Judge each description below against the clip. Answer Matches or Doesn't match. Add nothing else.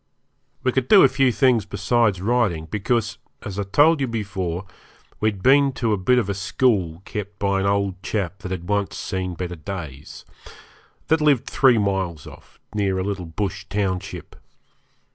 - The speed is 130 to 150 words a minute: Doesn't match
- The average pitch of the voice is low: Matches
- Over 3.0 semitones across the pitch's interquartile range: Matches